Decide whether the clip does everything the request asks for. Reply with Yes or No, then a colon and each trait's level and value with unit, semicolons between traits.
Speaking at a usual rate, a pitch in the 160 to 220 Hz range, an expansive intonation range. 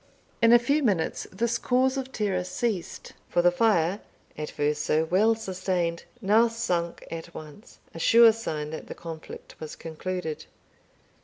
Yes: average, 155 wpm; medium, 185 Hz; wide, 5.7 semitones